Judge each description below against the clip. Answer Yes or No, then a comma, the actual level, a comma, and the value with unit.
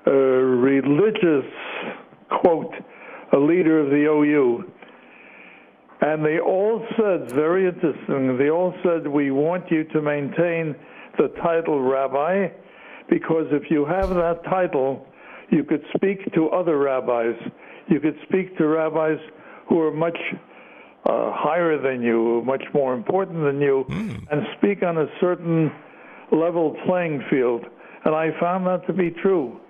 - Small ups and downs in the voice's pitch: No, average, 4.0 semitones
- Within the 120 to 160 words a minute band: Yes, average, 140 wpm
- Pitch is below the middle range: No, medium, 160 Hz